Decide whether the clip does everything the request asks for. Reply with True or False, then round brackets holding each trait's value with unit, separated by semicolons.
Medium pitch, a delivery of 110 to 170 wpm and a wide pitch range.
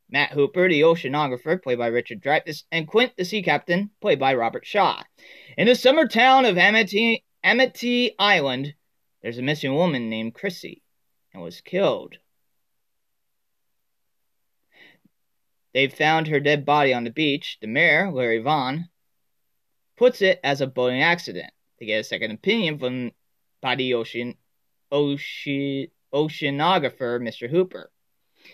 True (150 Hz; 135 wpm; 6.7 semitones)